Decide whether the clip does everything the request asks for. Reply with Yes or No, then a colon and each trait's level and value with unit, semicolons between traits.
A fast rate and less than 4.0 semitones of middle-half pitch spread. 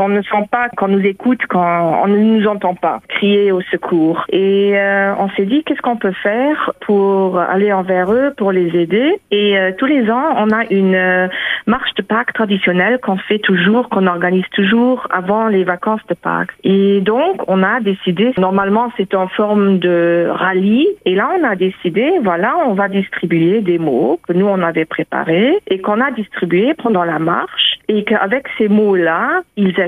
Yes: fast, 190 wpm; average, 3.2 semitones